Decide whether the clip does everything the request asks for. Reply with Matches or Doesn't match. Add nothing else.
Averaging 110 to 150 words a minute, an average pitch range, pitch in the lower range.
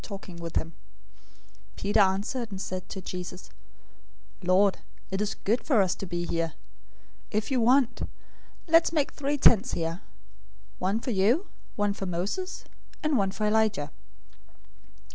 Doesn't match